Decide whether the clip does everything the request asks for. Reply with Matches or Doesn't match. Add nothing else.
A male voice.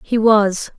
Doesn't match